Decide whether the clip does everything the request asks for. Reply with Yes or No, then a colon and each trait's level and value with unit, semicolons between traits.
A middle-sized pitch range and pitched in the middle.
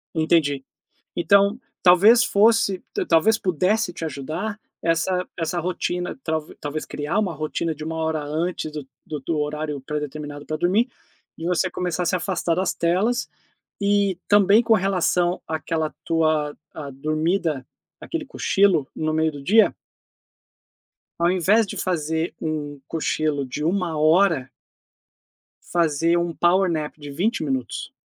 Yes: average, 3.4 semitones; medium, 165 Hz